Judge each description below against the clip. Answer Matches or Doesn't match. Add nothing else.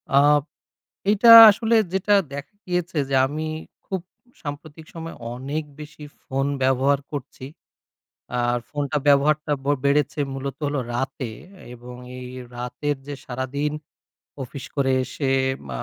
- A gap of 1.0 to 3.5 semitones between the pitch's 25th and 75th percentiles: Matches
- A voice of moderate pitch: Matches